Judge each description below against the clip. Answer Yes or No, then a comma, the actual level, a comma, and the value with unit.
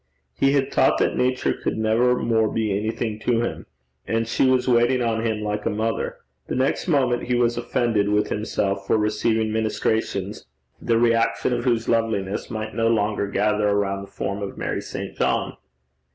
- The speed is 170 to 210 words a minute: Yes, average, 180 wpm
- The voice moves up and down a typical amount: No, narrow, 2.1 semitones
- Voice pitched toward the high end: No, low, 110 Hz